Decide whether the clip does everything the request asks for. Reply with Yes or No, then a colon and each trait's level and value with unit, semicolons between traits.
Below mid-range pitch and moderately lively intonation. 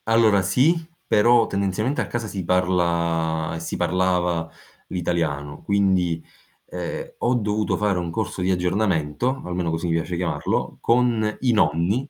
Yes: very low, 90 Hz; average, 4.3 semitones